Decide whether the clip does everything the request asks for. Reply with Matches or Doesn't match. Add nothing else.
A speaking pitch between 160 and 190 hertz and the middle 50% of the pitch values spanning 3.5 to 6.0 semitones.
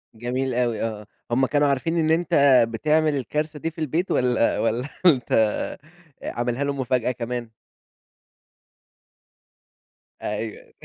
Doesn't match